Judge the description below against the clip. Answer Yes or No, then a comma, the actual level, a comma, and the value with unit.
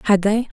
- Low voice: No, high, 210 Hz